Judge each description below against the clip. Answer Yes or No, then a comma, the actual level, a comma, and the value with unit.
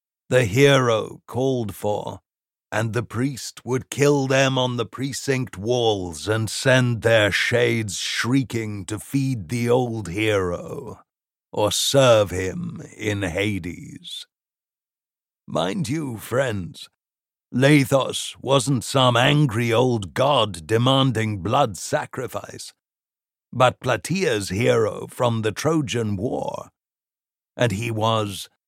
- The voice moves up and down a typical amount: Yes, average, 3.7 semitones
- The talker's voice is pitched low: Yes, low, 120 Hz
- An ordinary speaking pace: No, slow, 105 wpm